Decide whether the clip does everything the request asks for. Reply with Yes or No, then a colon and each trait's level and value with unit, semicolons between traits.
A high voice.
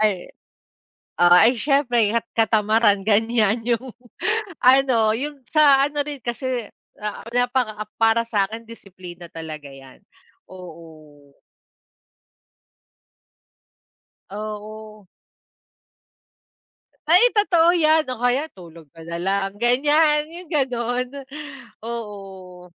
Yes: high, 225 Hz